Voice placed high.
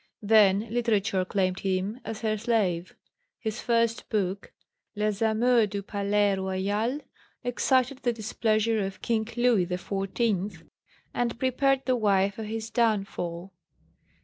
Yes: high, 215 Hz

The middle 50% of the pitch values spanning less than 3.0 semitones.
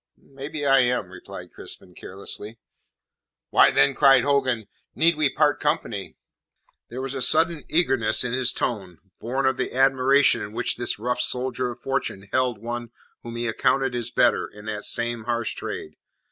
Yes: narrow, 2.5 semitones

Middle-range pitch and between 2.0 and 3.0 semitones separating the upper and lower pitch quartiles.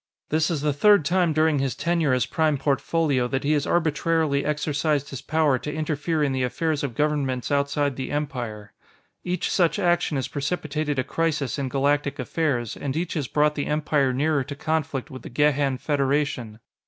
Yes: medium, 145 Hz; narrow, 2.4 semitones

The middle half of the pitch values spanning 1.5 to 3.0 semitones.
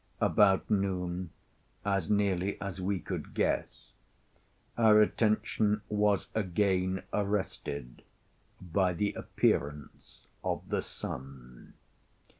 Yes: average, 2.7 semitones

